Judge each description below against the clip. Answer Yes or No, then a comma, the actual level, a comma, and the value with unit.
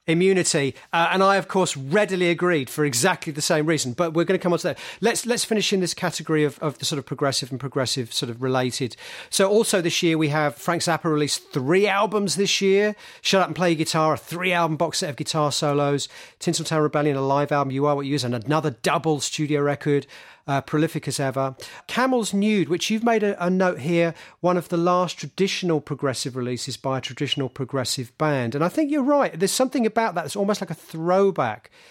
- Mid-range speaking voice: Yes, medium, 160 Hz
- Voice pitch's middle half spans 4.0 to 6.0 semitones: Yes, average, 4.6 semitones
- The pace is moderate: No, fast, 225 wpm